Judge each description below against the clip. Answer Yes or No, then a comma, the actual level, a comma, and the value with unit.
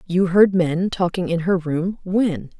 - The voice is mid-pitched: Yes, medium, 180 Hz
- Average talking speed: Yes, average, 160 wpm